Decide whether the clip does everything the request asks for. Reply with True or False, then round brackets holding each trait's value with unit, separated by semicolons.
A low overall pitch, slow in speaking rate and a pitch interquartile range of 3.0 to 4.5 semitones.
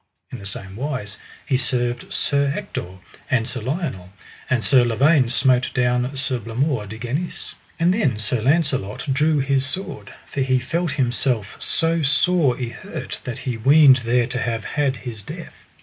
False (130 Hz; 165 wpm; 3.3 semitones)